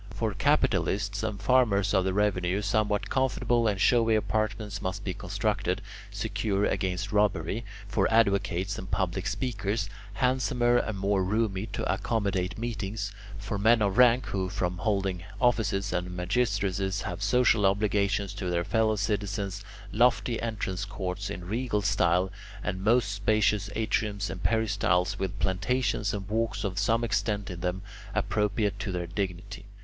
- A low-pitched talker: Yes, low, 100 Hz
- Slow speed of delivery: No, average, 145 wpm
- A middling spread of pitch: No, narrow, 2.3 semitones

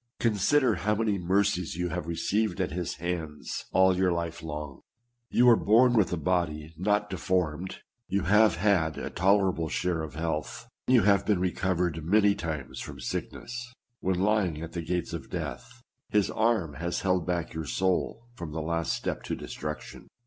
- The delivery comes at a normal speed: Yes, average, 175 wpm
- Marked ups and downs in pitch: No, average, 3.8 semitones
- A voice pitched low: Yes, very low, 90 Hz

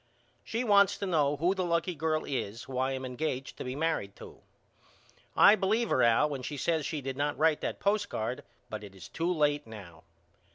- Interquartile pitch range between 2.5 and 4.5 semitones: No, average, 5.3 semitones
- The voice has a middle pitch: Yes, medium, 145 Hz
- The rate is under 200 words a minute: No, fast, 205 wpm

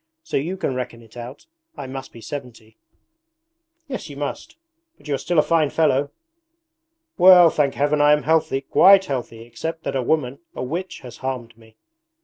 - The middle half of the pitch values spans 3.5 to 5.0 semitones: Yes, average, 4.4 semitones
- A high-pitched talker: No, medium, 140 Hz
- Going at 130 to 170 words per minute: No, average, 180 wpm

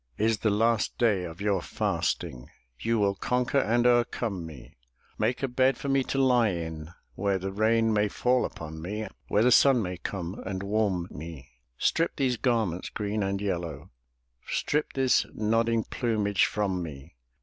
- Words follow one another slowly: No, average, 165 wpm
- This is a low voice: Yes, low, 105 Hz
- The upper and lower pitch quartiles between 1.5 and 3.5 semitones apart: No, average, 4.5 semitones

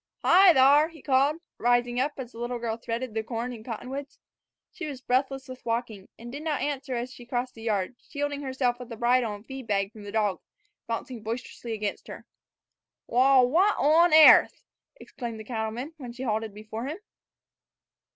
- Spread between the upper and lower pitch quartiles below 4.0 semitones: Yes, average, 3.2 semitones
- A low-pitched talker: No, high, 245 Hz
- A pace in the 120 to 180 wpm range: No, average, 190 wpm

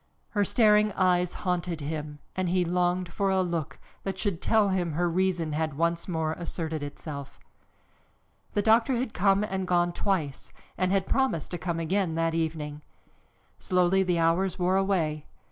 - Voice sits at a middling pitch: Yes, medium, 175 Hz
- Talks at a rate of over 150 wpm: Yes, average, 160 wpm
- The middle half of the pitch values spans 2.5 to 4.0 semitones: Yes, average, 2.8 semitones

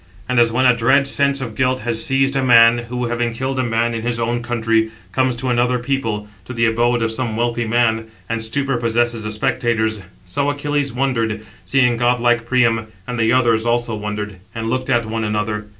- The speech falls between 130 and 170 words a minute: No, fast, 205 wpm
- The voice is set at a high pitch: No, low, 120 Hz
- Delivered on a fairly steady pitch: Yes, narrow, 2.1 semitones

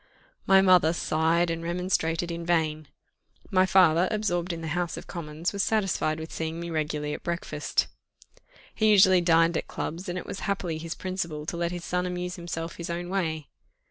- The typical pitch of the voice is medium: Yes, medium, 170 Hz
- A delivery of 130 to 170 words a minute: No, average, 185 wpm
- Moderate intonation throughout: No, narrow, 1.9 semitones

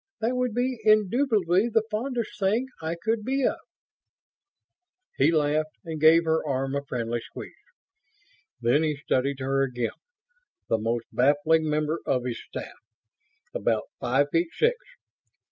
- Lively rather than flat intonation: Yes, wide, 7.9 semitones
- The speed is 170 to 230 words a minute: No, average, 140 wpm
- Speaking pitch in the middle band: Yes, medium, 160 Hz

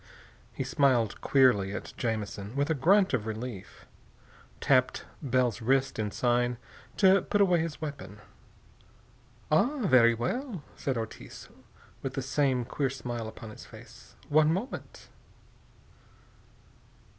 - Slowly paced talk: Yes, slow, 120 wpm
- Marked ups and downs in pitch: No, average, 4.7 semitones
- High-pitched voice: No, low, 130 Hz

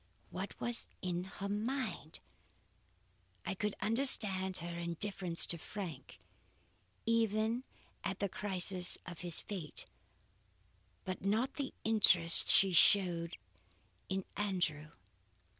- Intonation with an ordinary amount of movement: Yes, average, 3.3 semitones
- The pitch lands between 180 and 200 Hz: Yes, high, 190 Hz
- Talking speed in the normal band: No, slow, 105 wpm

